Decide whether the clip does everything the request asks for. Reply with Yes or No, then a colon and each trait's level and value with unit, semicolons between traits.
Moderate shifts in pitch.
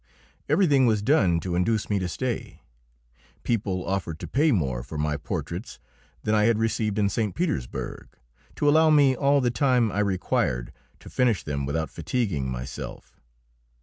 No: wide, 7.4 semitones